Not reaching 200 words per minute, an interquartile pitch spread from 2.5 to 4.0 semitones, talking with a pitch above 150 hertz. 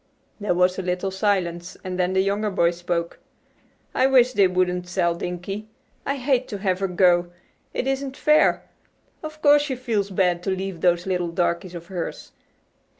Yes: average, 175 wpm; average, 3.3 semitones; medium, 185 Hz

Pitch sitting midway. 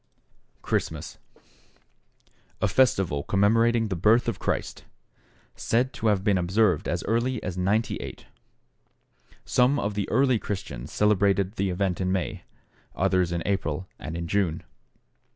No: low, 100 Hz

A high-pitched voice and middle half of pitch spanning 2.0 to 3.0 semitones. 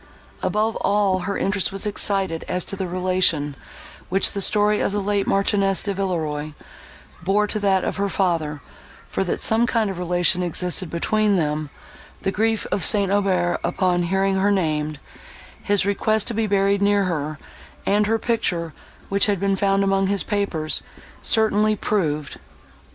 Yes: high, 195 Hz; narrow, 2.5 semitones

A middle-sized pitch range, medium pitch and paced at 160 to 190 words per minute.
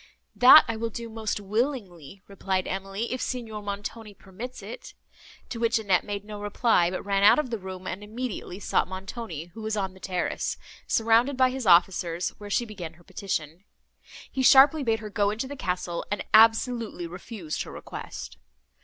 No: average, 3.6 semitones; high, 205 Hz; average, 180 wpm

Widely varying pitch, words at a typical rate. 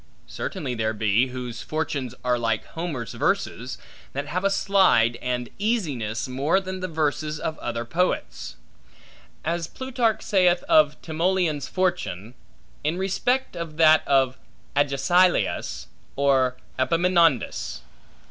No: wide, 6.1 semitones; slow, 120 wpm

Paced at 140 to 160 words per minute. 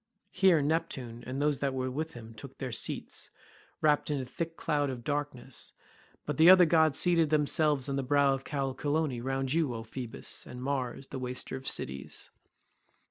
No: average, 180 wpm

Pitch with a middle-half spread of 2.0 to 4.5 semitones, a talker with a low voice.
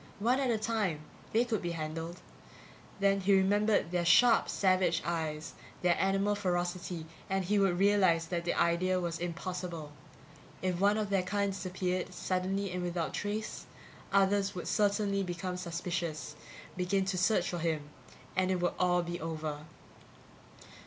No: narrow, 2.5 semitones; medium, 185 Hz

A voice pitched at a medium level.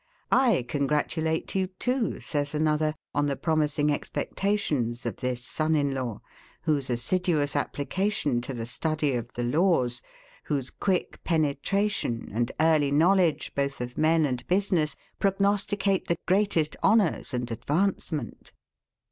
Yes: medium, 155 Hz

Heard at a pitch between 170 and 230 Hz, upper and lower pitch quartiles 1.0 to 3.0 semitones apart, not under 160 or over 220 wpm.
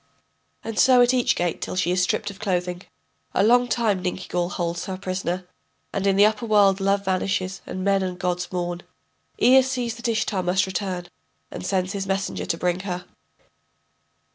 Yes: high, 190 Hz; narrow, 2.4 semitones; average, 180 wpm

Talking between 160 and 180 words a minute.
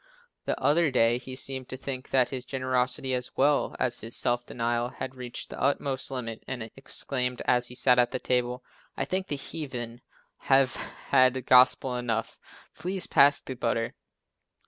Yes: average, 170 wpm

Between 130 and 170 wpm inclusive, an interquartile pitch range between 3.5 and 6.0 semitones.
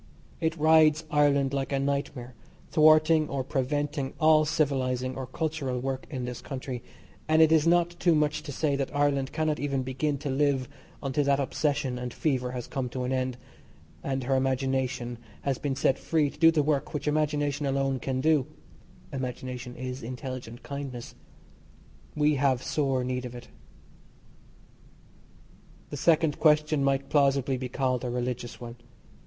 No: average, 160 wpm; average, 2.7 semitones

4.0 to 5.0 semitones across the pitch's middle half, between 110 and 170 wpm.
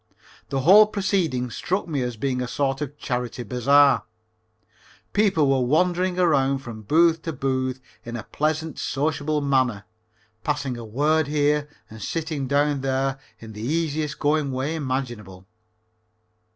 No: average, 3.4 semitones; average, 140 wpm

